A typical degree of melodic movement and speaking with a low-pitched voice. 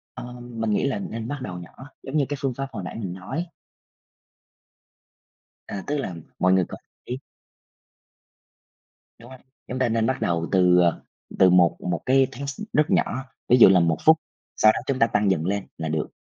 No: wide, 6.4 semitones; low, 115 Hz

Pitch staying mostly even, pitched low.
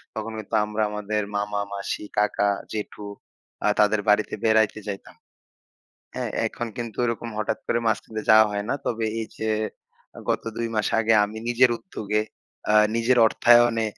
Yes: narrow, 1.6 semitones; low, 110 Hz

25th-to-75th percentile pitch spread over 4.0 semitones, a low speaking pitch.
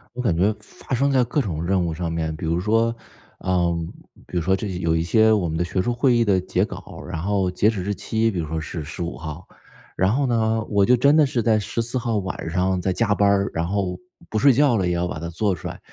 Yes: average, 4.6 semitones; very low, 95 Hz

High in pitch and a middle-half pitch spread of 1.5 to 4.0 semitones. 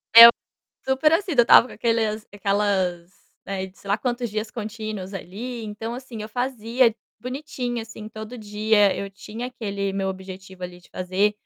Yes: high, 215 Hz; average, 3.3 semitones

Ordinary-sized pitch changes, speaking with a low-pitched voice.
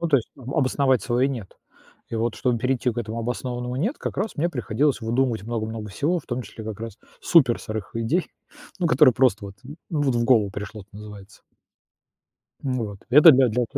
Yes: average, 3.4 semitones; low, 120 Hz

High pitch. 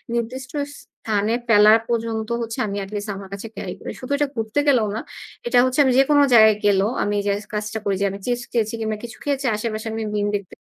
Yes: high, 220 Hz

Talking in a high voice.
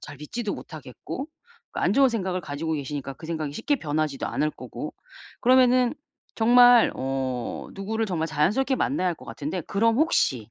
No: medium, 180 Hz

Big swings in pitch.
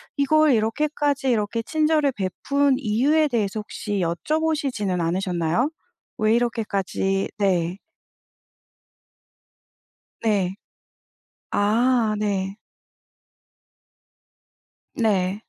Yes: wide, 6.2 semitones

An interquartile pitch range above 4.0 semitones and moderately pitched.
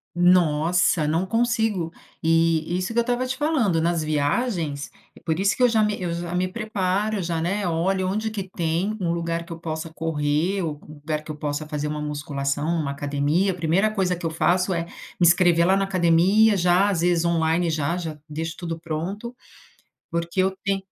No: average, 3.2 semitones; medium, 170 Hz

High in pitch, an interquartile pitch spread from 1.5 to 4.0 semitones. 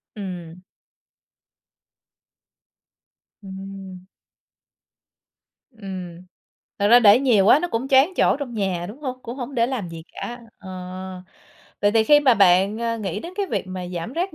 No: high, 210 Hz; average, 5.1 semitones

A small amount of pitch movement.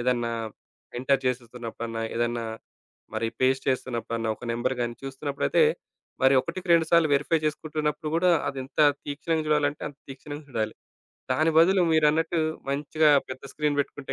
No: average, 3.8 semitones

